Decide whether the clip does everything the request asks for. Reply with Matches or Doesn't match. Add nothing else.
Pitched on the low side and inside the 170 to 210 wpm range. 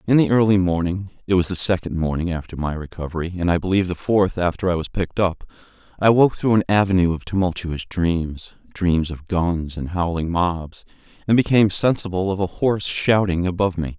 Matches